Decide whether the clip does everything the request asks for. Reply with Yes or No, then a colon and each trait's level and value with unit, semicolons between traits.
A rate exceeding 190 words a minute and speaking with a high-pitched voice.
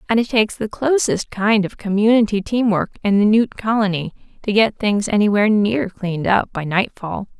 No: average, 185 wpm; high, 210 Hz